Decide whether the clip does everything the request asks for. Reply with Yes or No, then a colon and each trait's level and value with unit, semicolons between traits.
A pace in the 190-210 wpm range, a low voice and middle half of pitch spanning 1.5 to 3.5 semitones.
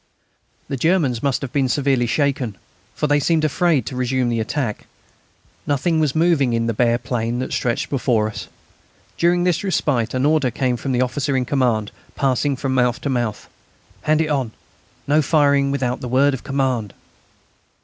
No: average, 175 wpm; low, 130 Hz; average, 3.1 semitones